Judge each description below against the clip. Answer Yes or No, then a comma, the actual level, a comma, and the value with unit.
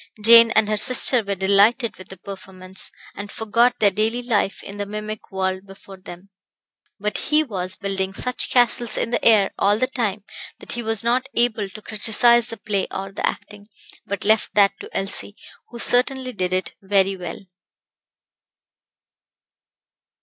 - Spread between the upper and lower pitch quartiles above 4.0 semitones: No, average, 3.2 semitones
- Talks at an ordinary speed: Yes, average, 165 wpm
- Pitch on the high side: Yes, high, 210 Hz